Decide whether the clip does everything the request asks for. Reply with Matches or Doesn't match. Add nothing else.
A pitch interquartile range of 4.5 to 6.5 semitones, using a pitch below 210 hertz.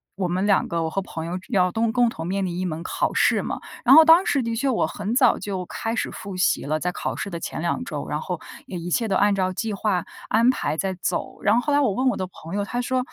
Matches